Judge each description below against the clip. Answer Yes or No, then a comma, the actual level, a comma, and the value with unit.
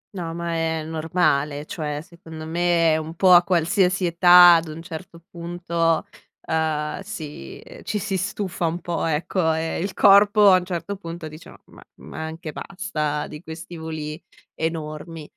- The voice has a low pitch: No, medium, 165 Hz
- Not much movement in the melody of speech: Yes, narrow, 2.0 semitones